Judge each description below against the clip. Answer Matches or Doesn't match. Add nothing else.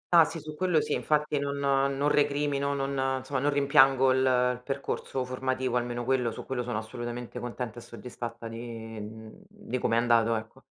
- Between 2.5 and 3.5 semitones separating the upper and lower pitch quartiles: Matches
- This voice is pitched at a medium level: Doesn't match